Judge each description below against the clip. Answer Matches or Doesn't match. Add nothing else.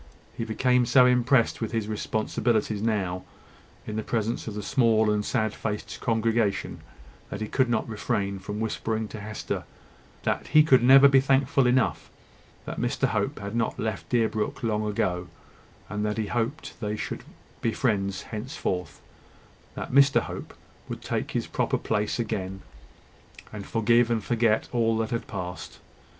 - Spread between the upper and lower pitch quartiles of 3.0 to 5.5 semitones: Doesn't match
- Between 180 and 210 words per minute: Doesn't match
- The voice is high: Doesn't match